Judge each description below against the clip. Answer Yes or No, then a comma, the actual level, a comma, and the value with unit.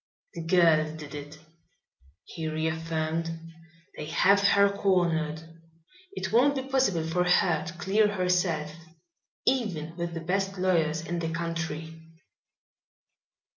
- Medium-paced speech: No, slow, 120 wpm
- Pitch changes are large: No, average, 2.9 semitones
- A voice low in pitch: No, medium, 165 Hz